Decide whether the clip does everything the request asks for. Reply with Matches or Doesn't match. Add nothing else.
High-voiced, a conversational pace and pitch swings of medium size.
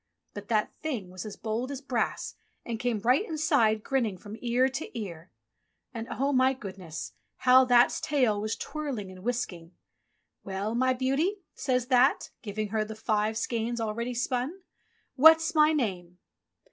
Matches